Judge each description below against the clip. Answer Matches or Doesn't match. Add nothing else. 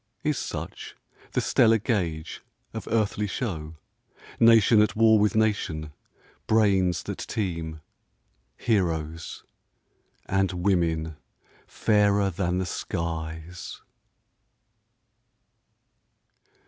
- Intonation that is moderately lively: Matches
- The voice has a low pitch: Matches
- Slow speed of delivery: Matches